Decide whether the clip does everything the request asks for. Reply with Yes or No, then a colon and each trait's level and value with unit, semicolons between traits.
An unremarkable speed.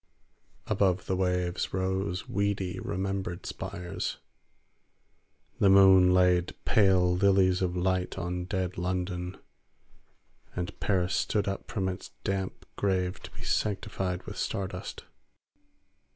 No: slow, 115 wpm